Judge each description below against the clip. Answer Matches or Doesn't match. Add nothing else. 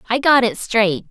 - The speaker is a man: Doesn't match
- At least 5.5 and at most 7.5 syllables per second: Doesn't match